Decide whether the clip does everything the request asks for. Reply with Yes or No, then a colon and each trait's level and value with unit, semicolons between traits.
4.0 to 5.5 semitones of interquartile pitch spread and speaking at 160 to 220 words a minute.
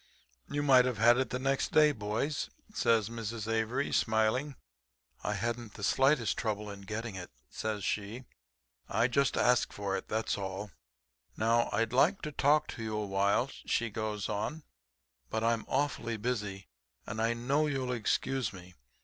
No: average, 3.6 semitones; average, 165 wpm